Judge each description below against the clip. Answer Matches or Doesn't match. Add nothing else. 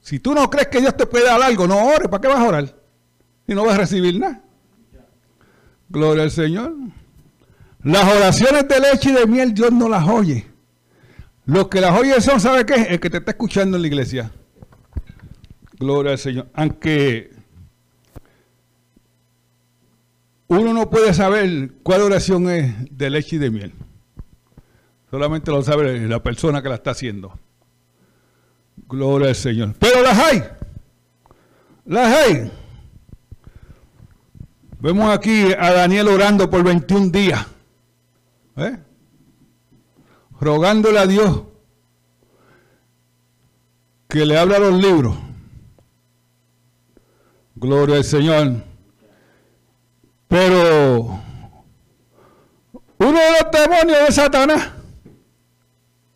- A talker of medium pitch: Matches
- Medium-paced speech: Doesn't match